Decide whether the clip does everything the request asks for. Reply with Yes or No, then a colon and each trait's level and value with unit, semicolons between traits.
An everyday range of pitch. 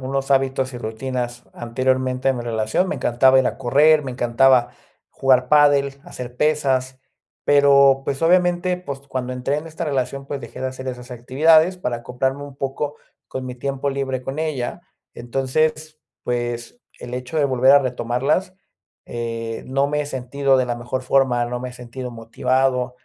No: narrow, 2.3 semitones